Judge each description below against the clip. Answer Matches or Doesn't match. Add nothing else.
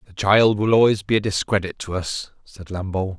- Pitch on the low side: Matches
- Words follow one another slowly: Doesn't match